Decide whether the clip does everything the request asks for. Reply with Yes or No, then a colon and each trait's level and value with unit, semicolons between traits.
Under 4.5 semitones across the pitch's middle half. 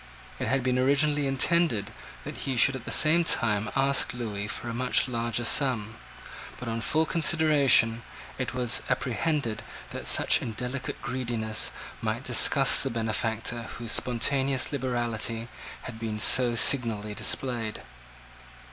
Yes: average, 3.1 semitones